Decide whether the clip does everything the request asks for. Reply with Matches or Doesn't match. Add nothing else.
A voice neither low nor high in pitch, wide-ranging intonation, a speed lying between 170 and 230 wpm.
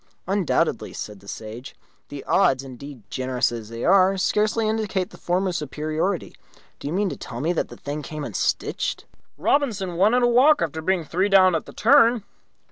Matches